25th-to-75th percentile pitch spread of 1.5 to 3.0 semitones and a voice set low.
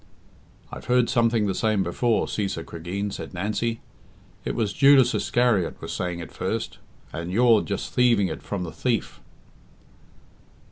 No: average, 4.5 semitones; low, 105 Hz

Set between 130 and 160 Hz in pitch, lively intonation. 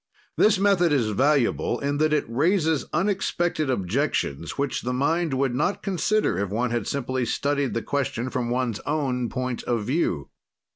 No: low, 135 Hz; average, 4.4 semitones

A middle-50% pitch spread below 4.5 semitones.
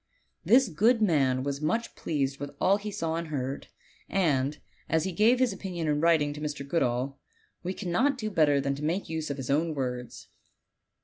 No: average, 5.3 semitones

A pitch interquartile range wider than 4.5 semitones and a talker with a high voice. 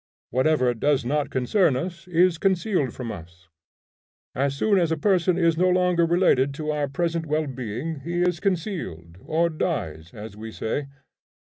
No: wide, 5.4 semitones; medium, 155 Hz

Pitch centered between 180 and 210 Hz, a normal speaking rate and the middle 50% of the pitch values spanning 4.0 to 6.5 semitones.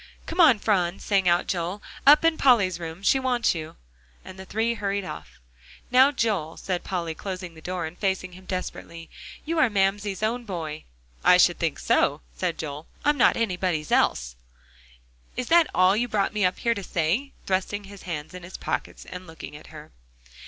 Yes: high, 190 Hz; average, 190 wpm; average, 4.5 semitones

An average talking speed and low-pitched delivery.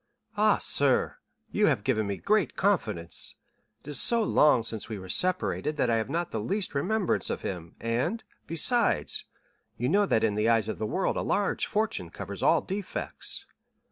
Yes: average, 175 wpm; low, 130 Hz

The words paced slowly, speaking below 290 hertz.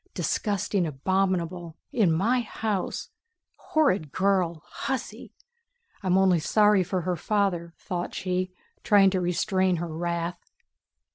Yes: slow, 115 wpm; medium, 185 Hz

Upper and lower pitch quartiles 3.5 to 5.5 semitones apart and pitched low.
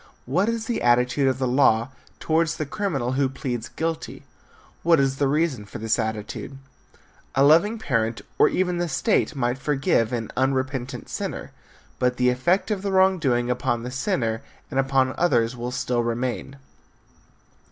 Yes: average, 5.0 semitones; low, 130 Hz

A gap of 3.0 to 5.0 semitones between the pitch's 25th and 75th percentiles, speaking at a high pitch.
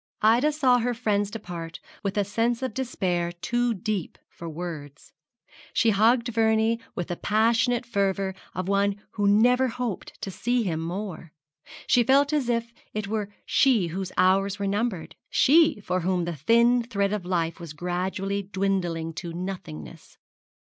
Yes: average, 4.6 semitones; high, 200 Hz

